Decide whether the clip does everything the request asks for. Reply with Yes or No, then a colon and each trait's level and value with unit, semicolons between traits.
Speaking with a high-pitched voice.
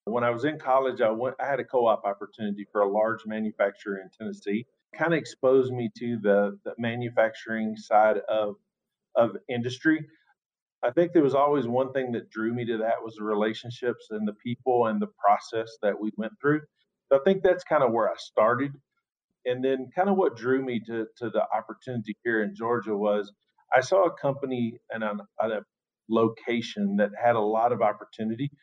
No: low, 120 Hz